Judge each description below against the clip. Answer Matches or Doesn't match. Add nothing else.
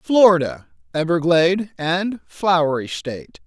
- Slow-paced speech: Matches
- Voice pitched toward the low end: Doesn't match